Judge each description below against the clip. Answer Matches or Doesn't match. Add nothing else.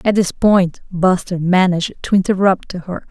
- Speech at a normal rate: Matches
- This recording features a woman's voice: Matches